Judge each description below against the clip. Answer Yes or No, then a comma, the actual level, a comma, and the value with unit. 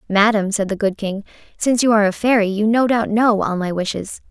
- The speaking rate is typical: No, fast, 235 wpm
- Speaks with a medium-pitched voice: No, high, 210 Hz